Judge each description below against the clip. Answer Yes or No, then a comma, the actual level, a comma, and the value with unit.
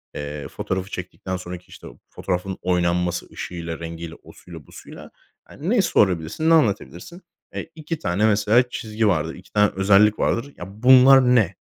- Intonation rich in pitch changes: Yes, wide, 5.8 semitones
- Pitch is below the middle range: Yes, very low, 95 Hz